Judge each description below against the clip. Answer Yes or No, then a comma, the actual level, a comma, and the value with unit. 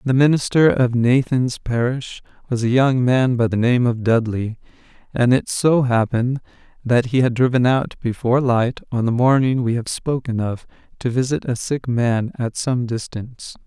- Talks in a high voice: No, low, 125 Hz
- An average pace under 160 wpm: No, average, 175 wpm